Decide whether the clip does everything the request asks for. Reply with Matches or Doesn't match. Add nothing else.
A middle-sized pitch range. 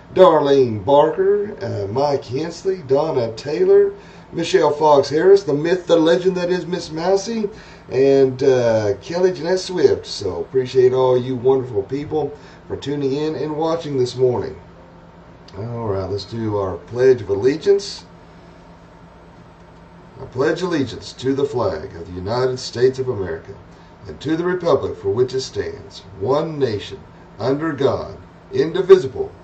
Doesn't match